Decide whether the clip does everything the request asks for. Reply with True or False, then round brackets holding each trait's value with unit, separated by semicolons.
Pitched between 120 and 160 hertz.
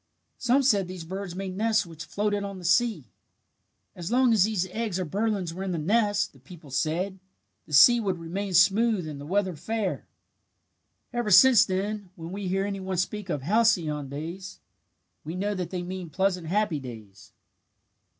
False (190 Hz)